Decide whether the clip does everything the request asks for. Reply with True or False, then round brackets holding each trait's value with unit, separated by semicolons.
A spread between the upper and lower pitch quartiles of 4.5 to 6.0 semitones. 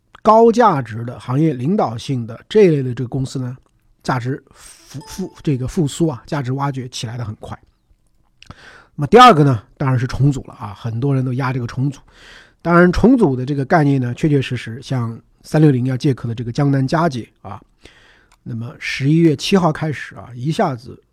False (4.1 semitones)